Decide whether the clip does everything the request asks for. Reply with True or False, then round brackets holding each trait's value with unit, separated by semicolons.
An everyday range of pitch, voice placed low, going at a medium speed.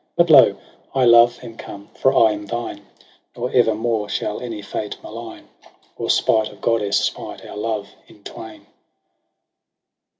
False (2.3 semitones; 110 Hz; 155 wpm)